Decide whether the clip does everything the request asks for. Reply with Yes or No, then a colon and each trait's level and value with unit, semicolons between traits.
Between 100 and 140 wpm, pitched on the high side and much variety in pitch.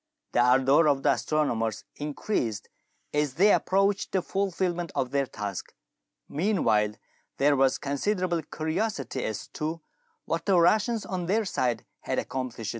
No: slow, 135 wpm; medium, 150 Hz; wide, 6.4 semitones